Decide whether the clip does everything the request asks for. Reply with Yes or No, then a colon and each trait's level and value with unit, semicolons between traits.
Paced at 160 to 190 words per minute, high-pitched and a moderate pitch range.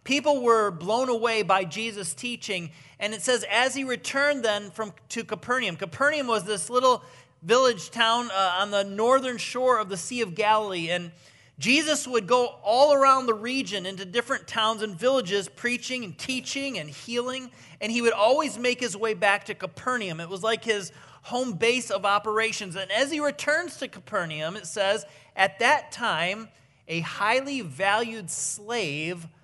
Yes: average, 170 wpm; high, 220 Hz; average, 4.4 semitones